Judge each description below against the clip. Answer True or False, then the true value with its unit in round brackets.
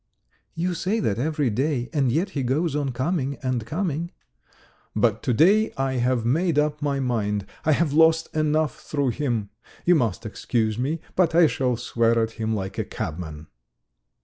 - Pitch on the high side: False (135 Hz)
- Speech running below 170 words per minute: False (175 wpm)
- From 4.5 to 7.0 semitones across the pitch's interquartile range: True (5.4 semitones)